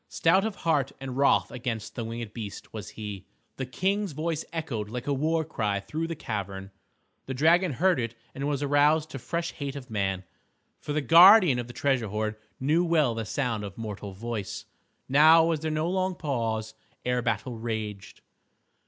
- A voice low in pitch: Yes, low, 130 Hz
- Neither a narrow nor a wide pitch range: No, wide, 6.2 semitones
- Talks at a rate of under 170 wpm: No, average, 180 wpm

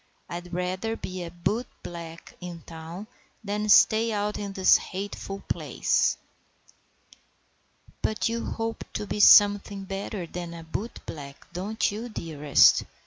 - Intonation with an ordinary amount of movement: Yes, average, 3.5 semitones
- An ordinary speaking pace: No, slow, 125 wpm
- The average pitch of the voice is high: Yes, high, 195 Hz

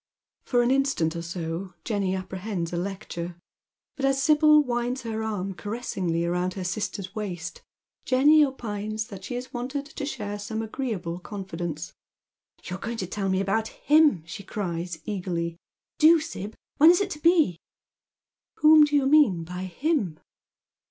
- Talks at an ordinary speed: Yes, average, 165 wpm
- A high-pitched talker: Yes, high, 205 Hz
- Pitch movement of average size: No, wide, 6.9 semitones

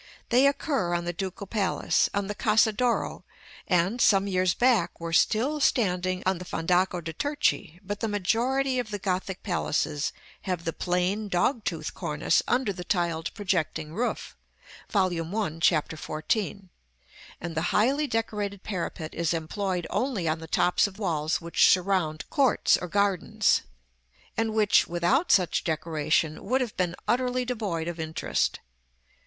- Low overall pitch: No, medium, 185 Hz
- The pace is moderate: Yes, average, 160 wpm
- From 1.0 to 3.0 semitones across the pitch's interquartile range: No, average, 4.5 semitones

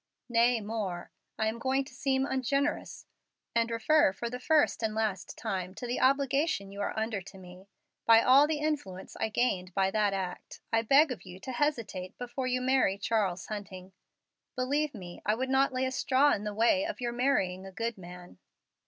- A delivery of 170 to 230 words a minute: Yes, average, 195 wpm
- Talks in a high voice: Yes, high, 230 Hz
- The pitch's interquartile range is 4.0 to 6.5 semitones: Yes, average, 5.3 semitones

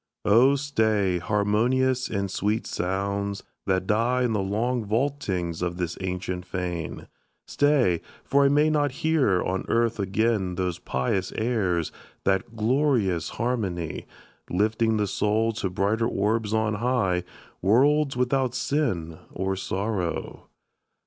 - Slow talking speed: Yes, slow, 125 wpm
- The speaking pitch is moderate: No, low, 105 Hz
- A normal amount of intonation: Yes, average, 4.8 semitones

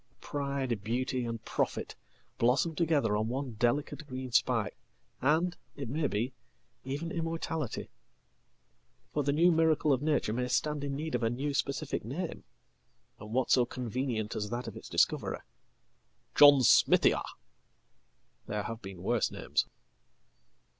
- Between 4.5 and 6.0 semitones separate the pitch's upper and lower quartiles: No, average, 3.9 semitones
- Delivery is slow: Yes, slow, 125 wpm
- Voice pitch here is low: Yes, low, 130 Hz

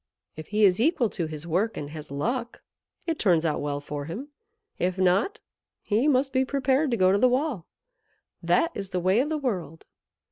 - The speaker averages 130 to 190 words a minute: No, average, 200 wpm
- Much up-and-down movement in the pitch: Yes, wide, 7.7 semitones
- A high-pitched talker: Yes, high, 205 Hz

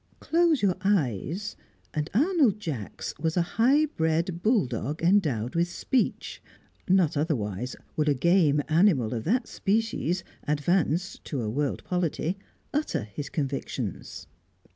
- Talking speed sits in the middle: No, slow, 125 wpm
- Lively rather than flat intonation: Yes, wide, 5.9 semitones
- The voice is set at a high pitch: No, medium, 170 Hz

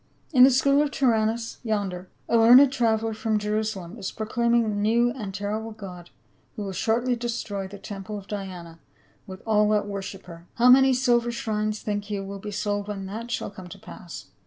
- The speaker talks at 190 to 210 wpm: Yes, average, 195 wpm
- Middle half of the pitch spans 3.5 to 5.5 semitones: No, average, 3.0 semitones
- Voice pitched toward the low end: No, high, 215 Hz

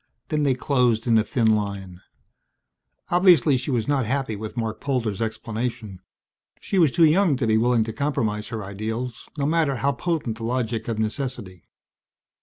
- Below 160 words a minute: No, average, 170 wpm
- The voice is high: No, low, 120 Hz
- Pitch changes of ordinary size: Yes, average, 4.2 semitones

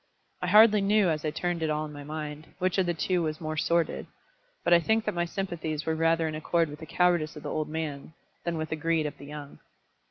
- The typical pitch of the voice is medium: Yes, medium, 160 Hz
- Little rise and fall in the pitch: Yes, narrow, 2.1 semitones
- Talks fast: Yes, fast, 255 wpm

